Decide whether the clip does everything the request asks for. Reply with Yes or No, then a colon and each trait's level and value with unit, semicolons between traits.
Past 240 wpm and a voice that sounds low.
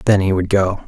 Yes: fast, 275 wpm; very low, 95 Hz